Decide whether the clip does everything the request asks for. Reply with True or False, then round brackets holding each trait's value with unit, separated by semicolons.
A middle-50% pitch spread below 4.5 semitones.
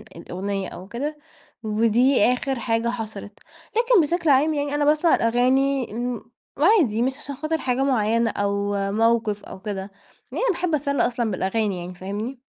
False (5.1 semitones)